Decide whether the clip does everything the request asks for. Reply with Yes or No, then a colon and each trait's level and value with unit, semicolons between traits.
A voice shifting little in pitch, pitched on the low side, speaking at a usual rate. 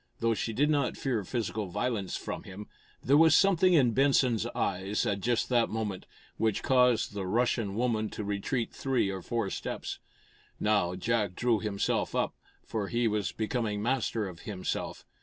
No: average, 3.5 semitones; low, 110 Hz; average, 165 wpm